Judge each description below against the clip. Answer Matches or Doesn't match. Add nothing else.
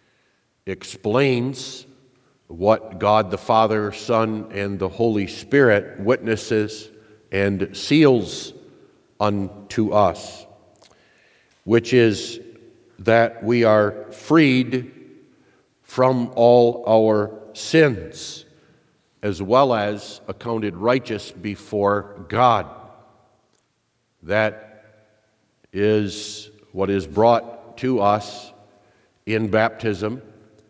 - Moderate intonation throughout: Matches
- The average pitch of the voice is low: Matches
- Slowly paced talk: Matches